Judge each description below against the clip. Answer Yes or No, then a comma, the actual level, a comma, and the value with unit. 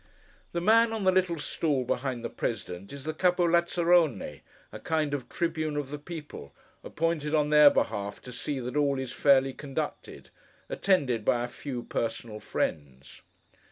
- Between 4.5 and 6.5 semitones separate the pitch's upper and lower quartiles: Yes, wide, 5.4 semitones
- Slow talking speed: No, average, 160 wpm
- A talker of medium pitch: Yes, medium, 145 Hz